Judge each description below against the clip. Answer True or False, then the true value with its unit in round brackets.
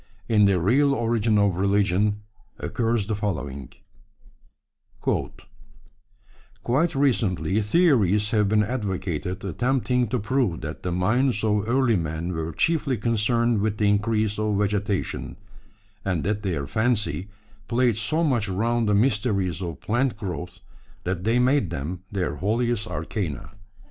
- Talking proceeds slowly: True (130 wpm)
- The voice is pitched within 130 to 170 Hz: False (105 Hz)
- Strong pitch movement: False (3.9 semitones)